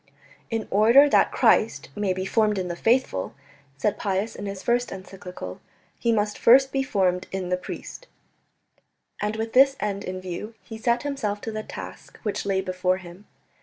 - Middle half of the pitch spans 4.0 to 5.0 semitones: No, average, 3.5 semitones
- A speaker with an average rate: Yes, average, 175 wpm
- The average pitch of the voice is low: No, high, 205 Hz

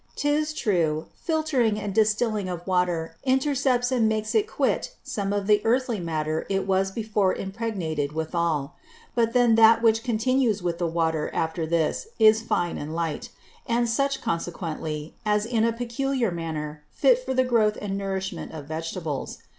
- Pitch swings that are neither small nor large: No, wide, 5.9 semitones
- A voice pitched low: No, high, 205 Hz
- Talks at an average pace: Yes, average, 160 wpm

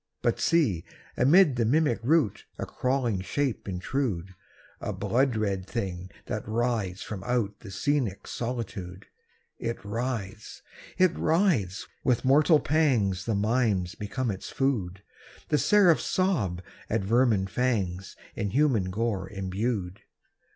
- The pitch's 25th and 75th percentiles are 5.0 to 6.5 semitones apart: Yes, wide, 5.4 semitones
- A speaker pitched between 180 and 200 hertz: No, low, 115 Hz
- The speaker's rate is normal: No, slow, 125 wpm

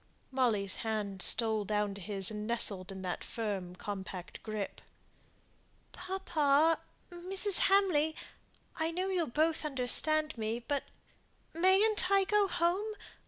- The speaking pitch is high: Yes, very high, 275 Hz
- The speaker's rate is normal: No, slow, 120 wpm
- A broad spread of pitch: Yes, wide, 9.0 semitones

